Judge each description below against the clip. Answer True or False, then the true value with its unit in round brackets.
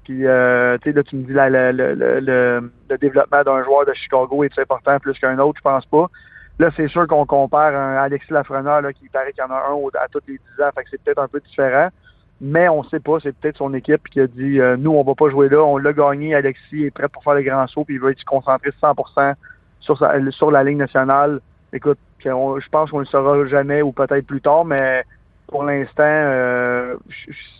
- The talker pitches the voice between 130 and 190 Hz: True (140 Hz)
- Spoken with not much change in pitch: True (1.5 semitones)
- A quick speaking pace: True (240 wpm)